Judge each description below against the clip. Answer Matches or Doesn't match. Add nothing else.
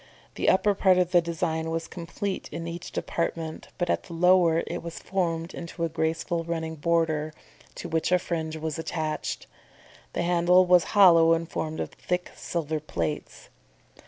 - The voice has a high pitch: Doesn't match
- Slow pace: Doesn't match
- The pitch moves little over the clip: Matches